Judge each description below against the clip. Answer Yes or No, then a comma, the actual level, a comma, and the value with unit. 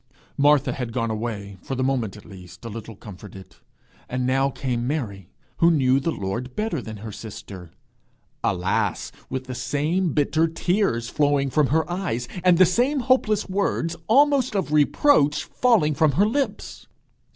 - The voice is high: No, medium, 140 Hz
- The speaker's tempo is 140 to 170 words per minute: Yes, average, 160 wpm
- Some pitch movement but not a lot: No, wide, 7.2 semitones